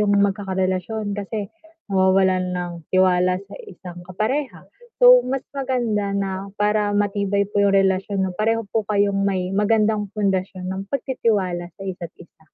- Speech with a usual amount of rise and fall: No, narrow, 2.1 semitones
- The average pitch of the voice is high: Yes, high, 200 Hz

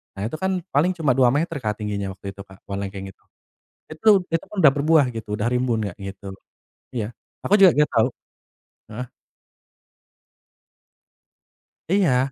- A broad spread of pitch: Yes, wide, 7.5 semitones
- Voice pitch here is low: Yes, low, 125 Hz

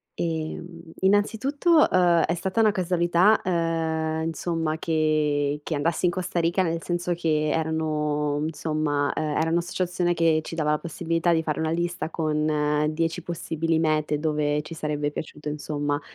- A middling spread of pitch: No, narrow, 2.2 semitones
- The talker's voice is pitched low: No, medium, 160 Hz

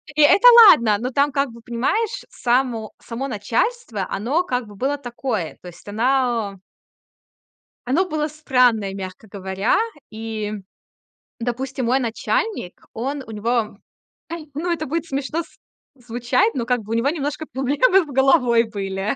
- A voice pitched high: Yes, very high, 250 Hz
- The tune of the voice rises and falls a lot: No, average, 4.6 semitones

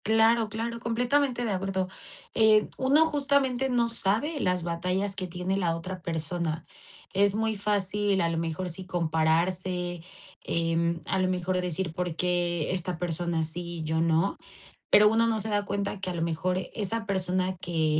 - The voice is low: No, medium, 185 Hz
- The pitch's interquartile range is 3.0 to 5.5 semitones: Yes, average, 4.0 semitones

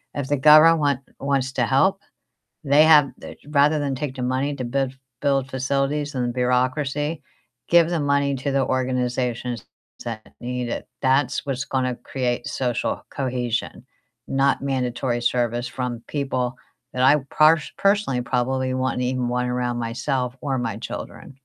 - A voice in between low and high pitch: No, low, 130 Hz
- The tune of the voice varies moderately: No, narrow, 2.3 semitones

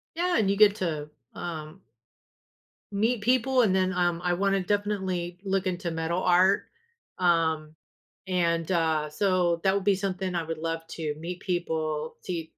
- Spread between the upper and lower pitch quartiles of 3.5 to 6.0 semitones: No, average, 3.0 semitones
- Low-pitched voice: No, medium, 180 Hz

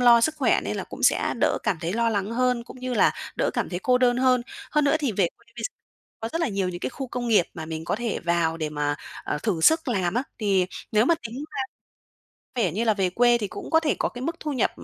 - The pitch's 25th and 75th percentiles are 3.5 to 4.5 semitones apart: No, wide, 5.4 semitones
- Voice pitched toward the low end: No, high, 230 Hz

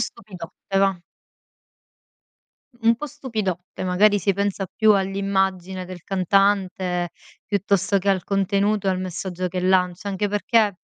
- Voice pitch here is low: No, high, 195 Hz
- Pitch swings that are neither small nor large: No, narrow, 1.8 semitones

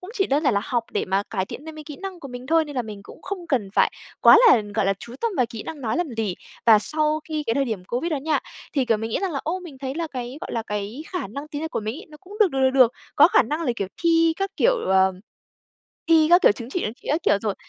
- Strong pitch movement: Yes, wide, 6.4 semitones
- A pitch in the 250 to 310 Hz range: Yes, very high, 275 Hz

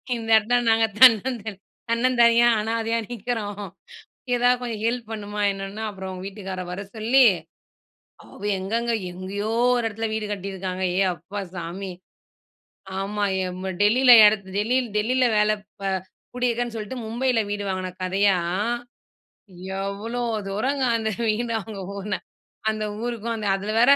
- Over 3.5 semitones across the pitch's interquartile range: No, average, 3.1 semitones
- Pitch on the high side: Yes, high, 215 Hz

